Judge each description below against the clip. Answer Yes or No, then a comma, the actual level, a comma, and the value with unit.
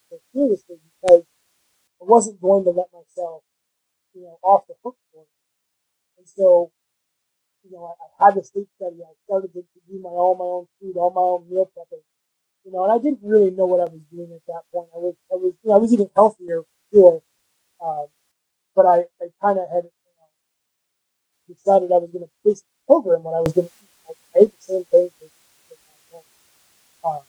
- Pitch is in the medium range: Yes, medium, 180 Hz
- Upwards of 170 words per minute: Yes, fast, 205 wpm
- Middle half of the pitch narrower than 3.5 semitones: Yes, narrow, 2.4 semitones